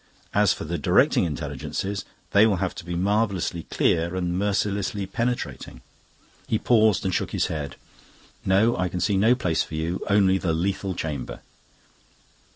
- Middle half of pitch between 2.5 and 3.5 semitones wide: Yes, average, 3.0 semitones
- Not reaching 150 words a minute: No, average, 165 wpm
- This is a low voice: Yes, very low, 95 Hz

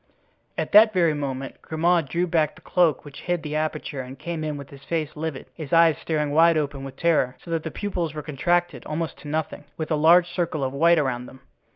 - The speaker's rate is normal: No, fast, 225 wpm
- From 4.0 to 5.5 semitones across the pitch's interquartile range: No, average, 2.8 semitones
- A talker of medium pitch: Yes, medium, 155 Hz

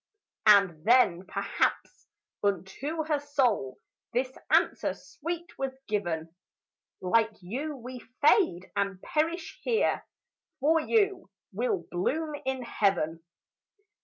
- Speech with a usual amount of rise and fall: No, wide, 8.2 semitones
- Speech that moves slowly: Yes, slow, 105 wpm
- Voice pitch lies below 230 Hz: No, very high, 255 Hz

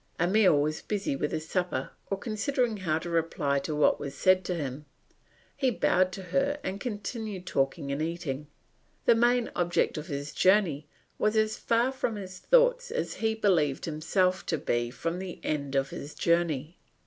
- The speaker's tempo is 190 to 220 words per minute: No, average, 175 wpm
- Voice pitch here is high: No, medium, 180 Hz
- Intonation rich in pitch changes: Yes, wide, 6.0 semitones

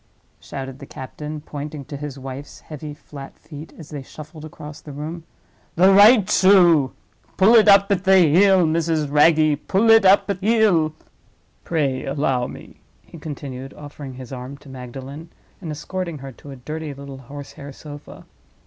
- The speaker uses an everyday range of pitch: Yes, average, 3.7 semitones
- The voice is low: No, medium, 150 Hz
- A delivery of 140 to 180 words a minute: Yes, average, 160 wpm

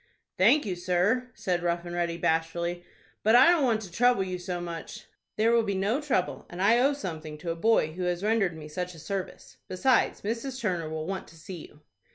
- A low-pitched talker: No, medium, 185 Hz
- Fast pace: Yes, fast, 215 wpm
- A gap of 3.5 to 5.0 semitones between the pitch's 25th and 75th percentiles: Yes, average, 4.7 semitones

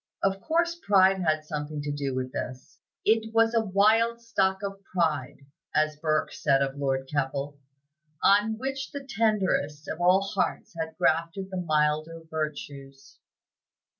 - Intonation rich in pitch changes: Yes, wide, 5.7 semitones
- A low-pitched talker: No, medium, 165 Hz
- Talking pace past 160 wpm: No, average, 145 wpm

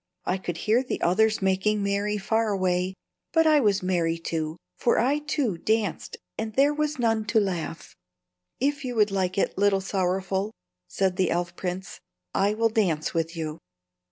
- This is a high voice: Yes, high, 195 Hz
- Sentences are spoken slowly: No, average, 170 wpm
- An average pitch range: Yes, average, 3.7 semitones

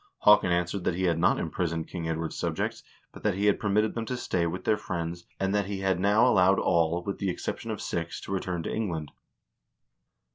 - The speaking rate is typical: No, fast, 220 wpm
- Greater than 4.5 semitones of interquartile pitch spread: No, average, 2.9 semitones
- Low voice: Yes, very low, 90 Hz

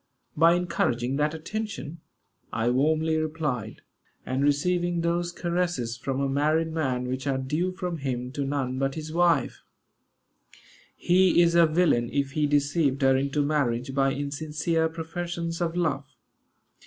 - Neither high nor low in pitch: Yes, medium, 150 Hz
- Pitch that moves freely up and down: No, average, 3.8 semitones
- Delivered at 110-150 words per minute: Yes, average, 140 wpm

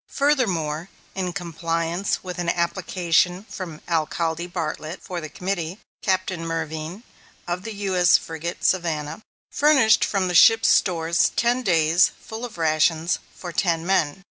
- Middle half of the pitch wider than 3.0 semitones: No, average, 2.7 semitones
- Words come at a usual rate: No, slow, 130 wpm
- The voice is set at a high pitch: No, medium, 175 Hz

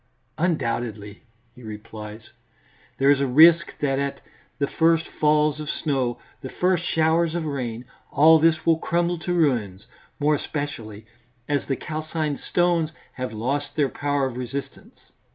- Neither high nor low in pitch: Yes, medium, 145 Hz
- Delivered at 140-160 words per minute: Yes, average, 145 wpm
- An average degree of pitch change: Yes, average, 4.3 semitones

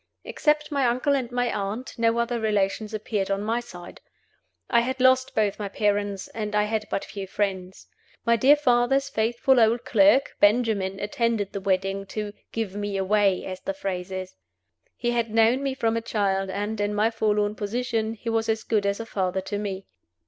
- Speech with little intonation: No, average, 3.0 semitones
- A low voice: No, high, 215 Hz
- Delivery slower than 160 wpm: No, average, 190 wpm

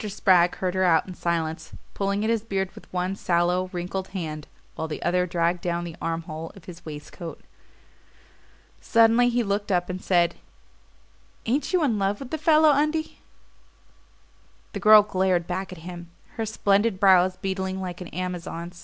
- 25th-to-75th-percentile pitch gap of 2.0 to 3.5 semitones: Yes, average, 2.9 semitones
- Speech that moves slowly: No, average, 165 wpm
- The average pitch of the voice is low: No, medium, 185 Hz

